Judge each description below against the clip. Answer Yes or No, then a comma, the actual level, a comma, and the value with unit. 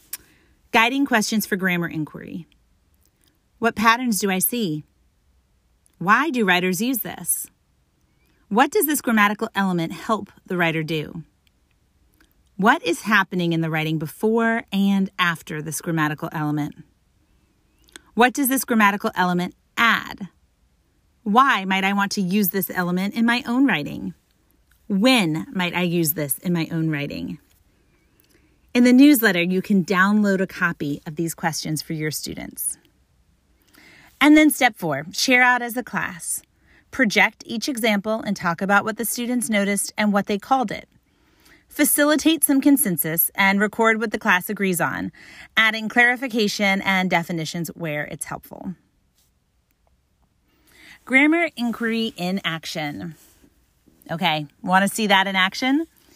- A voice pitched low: No, high, 195 Hz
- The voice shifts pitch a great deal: Yes, wide, 5.7 semitones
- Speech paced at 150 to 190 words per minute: No, average, 140 wpm